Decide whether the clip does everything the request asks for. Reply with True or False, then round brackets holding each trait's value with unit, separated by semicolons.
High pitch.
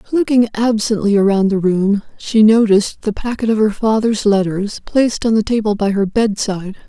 True (210 Hz)